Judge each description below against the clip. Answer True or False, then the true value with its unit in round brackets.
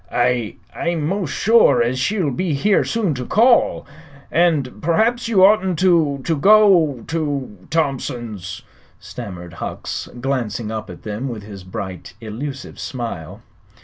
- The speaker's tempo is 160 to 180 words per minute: False (140 wpm)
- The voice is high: False (140 Hz)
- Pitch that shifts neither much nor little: False (7.7 semitones)